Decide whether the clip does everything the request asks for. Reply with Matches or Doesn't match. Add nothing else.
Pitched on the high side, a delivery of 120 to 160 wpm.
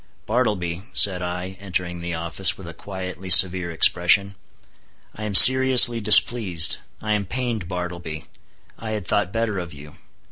Doesn't match